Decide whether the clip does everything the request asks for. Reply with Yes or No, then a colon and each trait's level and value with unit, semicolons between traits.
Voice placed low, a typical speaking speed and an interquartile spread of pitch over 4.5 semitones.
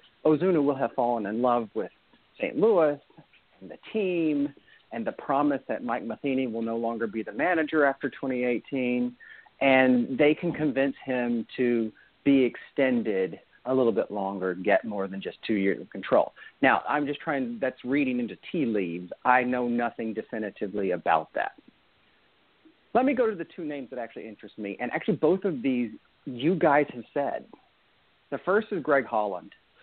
No: low, 125 Hz; average, 175 wpm; average, 3.9 semitones